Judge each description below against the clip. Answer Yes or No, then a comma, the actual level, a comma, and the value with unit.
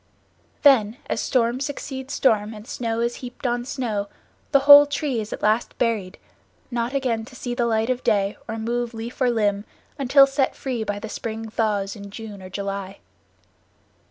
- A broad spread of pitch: No, average, 3.3 semitones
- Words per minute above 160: Yes, average, 180 wpm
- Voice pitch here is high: Yes, high, 230 Hz